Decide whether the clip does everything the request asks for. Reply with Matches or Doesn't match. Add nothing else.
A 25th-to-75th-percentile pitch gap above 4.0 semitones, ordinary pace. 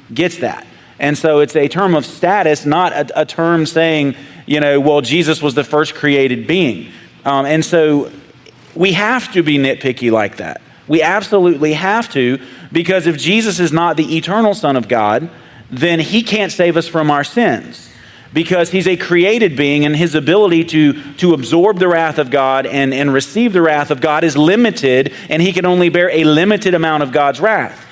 Doesn't match